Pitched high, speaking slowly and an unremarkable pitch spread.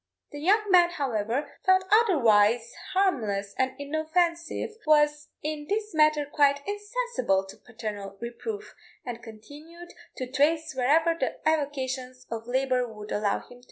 No: very high, 285 Hz; slow, 130 wpm; wide, 5.9 semitones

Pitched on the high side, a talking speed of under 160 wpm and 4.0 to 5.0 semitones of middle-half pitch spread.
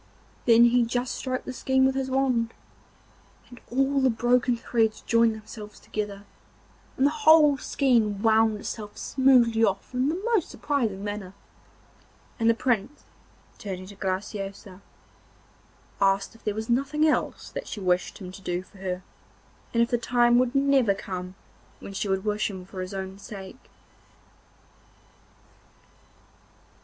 Yes: high, 225 Hz; average, 150 wpm; average, 4.5 semitones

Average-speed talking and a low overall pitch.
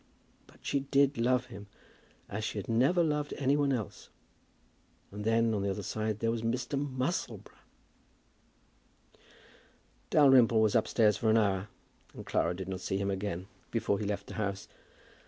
Yes: average, 160 wpm; low, 115 Hz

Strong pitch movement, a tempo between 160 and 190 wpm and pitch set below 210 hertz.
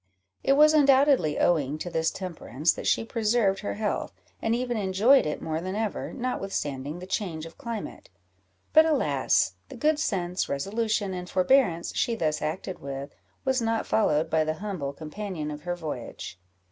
Yes: wide, 6.5 semitones; average, 165 wpm; high, 190 Hz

